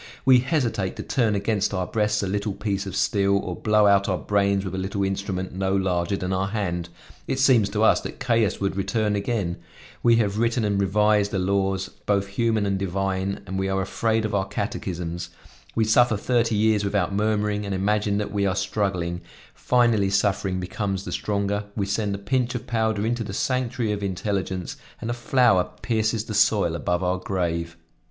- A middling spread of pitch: No, narrow, 2.2 semitones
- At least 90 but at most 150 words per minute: No, average, 190 wpm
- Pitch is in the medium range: No, low, 100 Hz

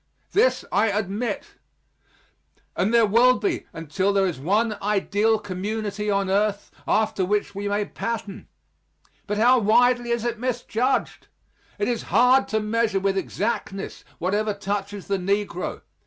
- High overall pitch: Yes, high, 210 Hz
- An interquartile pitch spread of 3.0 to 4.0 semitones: No, narrow, 2.6 semitones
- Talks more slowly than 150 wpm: Yes, average, 140 wpm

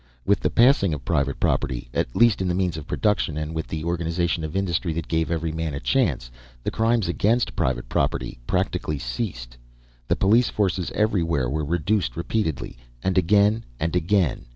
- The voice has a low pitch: Yes, very low, 85 Hz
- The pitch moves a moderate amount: Yes, average, 4.7 semitones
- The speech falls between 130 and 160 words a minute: No, average, 175 wpm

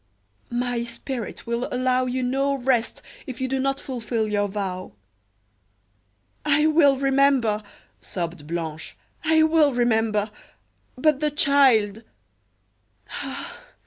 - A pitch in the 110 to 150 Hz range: No, high, 245 Hz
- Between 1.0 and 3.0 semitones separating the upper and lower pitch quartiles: No, average, 4.8 semitones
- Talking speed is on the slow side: Yes, slow, 115 wpm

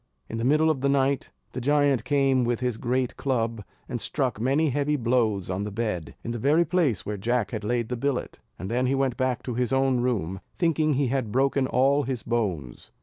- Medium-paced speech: No, fast, 215 wpm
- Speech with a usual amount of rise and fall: Yes, average, 3.3 semitones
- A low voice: Yes, low, 125 Hz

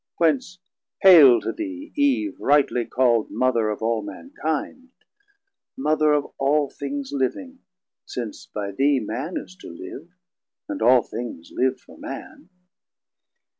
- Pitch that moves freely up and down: Yes, wide, 7.5 semitones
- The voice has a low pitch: No, medium, 145 Hz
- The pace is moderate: No, slow, 130 wpm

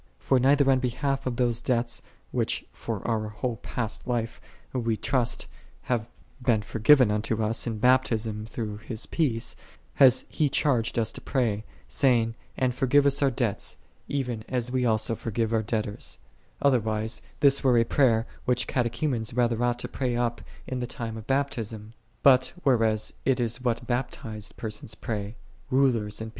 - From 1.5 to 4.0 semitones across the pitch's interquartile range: Yes, narrow, 2.5 semitones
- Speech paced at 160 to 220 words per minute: Yes, average, 175 wpm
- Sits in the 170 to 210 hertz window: No, low, 120 Hz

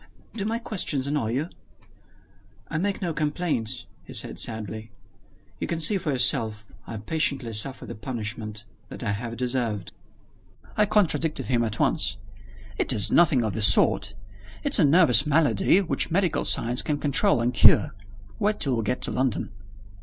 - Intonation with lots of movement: Yes, wide, 6.7 semitones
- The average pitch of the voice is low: Yes, low, 130 Hz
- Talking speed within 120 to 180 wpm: Yes, average, 160 wpm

